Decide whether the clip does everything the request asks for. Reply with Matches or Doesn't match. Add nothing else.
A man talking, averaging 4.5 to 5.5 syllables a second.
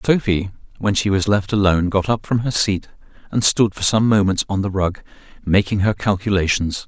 Matches